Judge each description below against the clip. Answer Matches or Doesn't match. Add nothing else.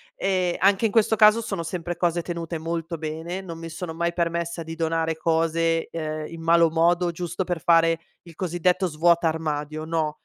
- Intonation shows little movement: Matches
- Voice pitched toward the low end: Doesn't match